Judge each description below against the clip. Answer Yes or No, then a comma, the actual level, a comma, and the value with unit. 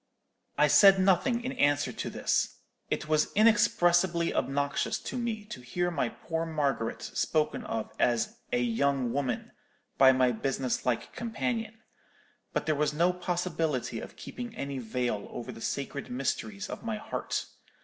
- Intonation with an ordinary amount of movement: No, wide, 6.7 semitones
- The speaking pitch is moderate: Yes, medium, 150 Hz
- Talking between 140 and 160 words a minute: Yes, average, 150 wpm